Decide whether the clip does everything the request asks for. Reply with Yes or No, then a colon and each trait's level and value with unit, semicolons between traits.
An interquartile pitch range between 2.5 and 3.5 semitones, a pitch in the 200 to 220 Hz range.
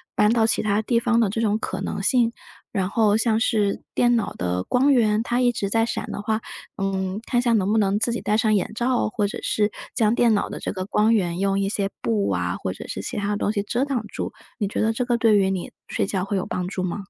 Yes: average, 2.9 semitones; high, 210 Hz